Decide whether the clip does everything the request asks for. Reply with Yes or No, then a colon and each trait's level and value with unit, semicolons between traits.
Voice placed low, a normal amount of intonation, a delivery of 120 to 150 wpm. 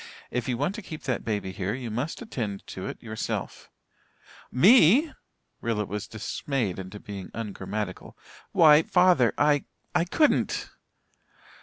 No: low, 120 Hz; wide, 7.5 semitones; slow, 135 wpm